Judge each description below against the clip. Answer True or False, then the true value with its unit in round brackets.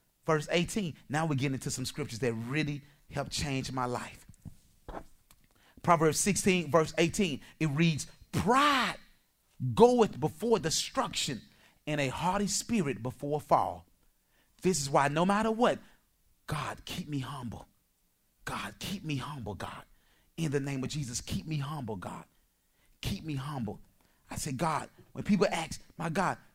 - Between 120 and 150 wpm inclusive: True (145 wpm)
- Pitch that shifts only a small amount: False (4.8 semitones)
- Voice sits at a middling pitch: True (145 Hz)